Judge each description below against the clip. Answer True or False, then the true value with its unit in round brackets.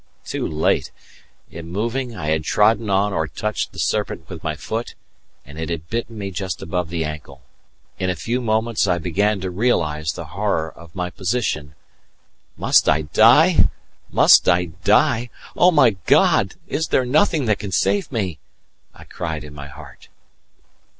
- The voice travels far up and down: True (6.0 semitones)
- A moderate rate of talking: True (165 wpm)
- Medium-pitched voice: False (95 Hz)